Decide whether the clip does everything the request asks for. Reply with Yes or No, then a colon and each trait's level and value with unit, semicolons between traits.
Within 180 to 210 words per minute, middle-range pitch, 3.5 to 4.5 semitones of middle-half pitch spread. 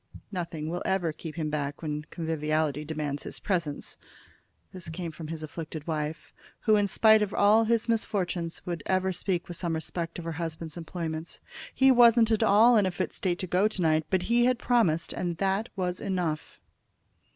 Yes: average, 185 wpm; medium, 175 Hz; average, 4.1 semitones